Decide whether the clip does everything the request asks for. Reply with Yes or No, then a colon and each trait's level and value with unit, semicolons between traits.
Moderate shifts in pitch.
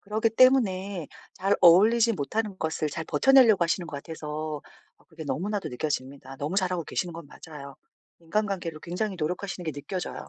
Yes: average, 4.7 semitones